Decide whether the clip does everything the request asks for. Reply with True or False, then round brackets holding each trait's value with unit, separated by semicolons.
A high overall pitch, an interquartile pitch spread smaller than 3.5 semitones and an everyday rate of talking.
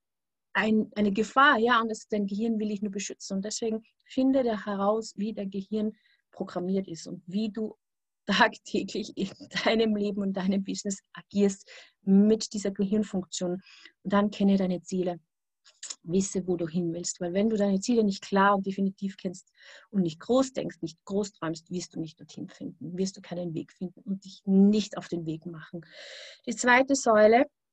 True (200 Hz; 2.8 semitones; 180 wpm)